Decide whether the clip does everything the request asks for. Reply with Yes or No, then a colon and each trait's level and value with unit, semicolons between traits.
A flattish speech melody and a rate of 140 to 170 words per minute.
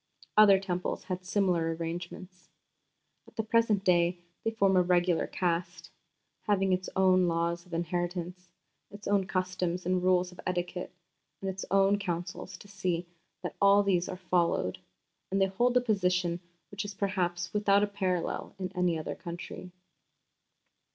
Yes: narrow, 1.9 semitones; average, 150 wpm